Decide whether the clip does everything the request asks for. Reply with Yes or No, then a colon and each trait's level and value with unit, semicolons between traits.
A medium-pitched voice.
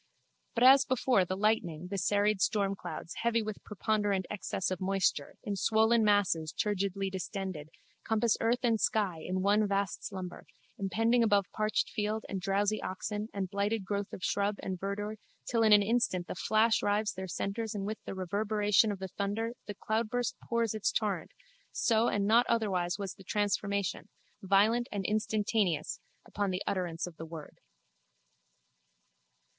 No: high, 205 Hz